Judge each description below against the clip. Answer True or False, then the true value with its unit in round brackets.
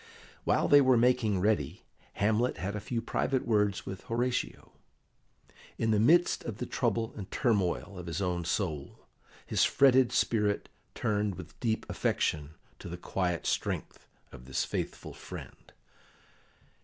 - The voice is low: True (105 Hz)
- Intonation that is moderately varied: True (4.5 semitones)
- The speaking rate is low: False (145 wpm)